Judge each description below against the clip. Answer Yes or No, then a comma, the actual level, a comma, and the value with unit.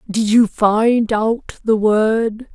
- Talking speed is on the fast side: No, average, 140 wpm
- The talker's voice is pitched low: No, high, 220 Hz